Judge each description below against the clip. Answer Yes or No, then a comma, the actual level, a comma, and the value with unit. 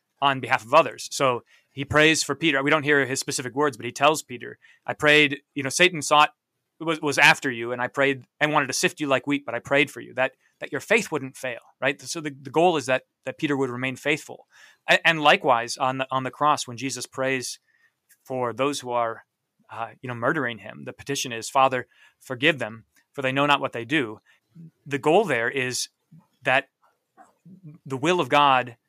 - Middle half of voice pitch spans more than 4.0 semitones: No, average, 3.0 semitones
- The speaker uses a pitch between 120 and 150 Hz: Yes, medium, 140 Hz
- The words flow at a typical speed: No, fast, 215 wpm